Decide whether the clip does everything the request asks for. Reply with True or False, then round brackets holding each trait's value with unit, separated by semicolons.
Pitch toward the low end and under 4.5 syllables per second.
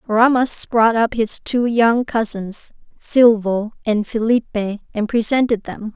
False (225 Hz; 4.0 syllables/s)